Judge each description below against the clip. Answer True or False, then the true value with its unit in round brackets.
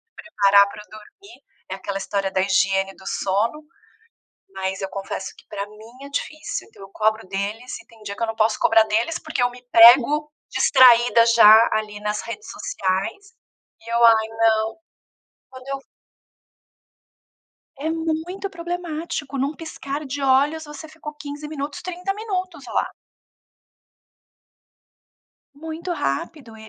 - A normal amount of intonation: False (6.4 semitones)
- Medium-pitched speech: False (245 Hz)